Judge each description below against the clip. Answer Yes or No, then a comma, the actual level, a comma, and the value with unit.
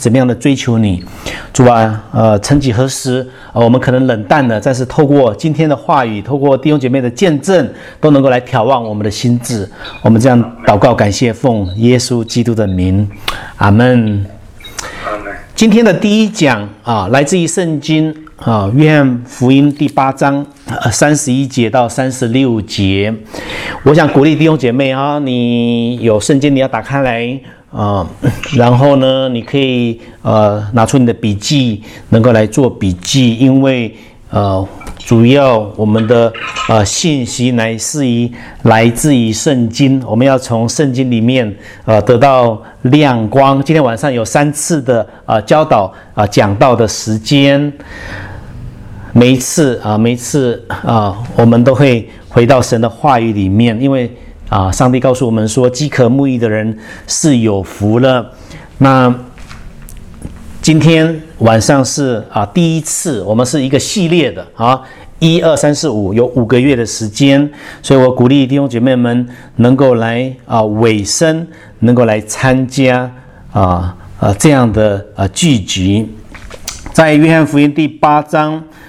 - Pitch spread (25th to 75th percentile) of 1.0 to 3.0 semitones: No, average, 4.1 semitones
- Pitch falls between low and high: No, low, 125 Hz